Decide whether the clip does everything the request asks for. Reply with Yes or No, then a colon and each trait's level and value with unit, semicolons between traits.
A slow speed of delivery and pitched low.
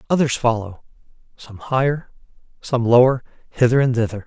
Yes: slow, 125 wpm; low, 120 Hz